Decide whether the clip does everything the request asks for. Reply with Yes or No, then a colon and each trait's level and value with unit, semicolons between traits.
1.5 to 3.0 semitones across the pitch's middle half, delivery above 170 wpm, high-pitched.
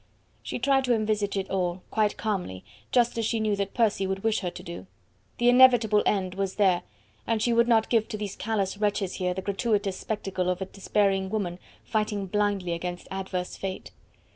Yes: narrow, 2.6 semitones; average, 190 wpm; high, 200 Hz